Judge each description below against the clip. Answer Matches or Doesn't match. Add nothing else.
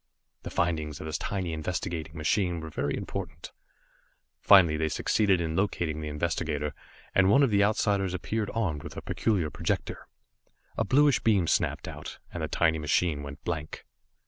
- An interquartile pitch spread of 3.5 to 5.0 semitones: Matches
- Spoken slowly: Doesn't match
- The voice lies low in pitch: Matches